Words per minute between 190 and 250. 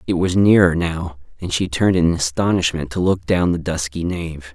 Yes: average, 200 wpm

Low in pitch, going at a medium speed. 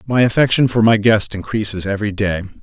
Yes: low, 105 Hz; average, 185 wpm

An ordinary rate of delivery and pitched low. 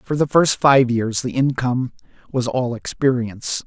Yes: average, 165 wpm; low, 125 Hz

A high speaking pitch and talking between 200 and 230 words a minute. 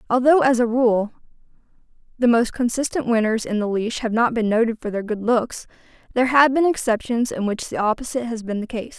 Yes: high, 235 Hz; fast, 205 wpm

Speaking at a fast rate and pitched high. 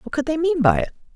Yes: fast, 315 wpm; very high, 305 Hz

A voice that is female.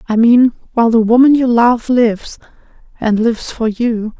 Yes: female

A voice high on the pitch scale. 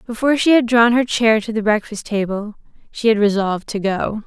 Yes: high, 220 Hz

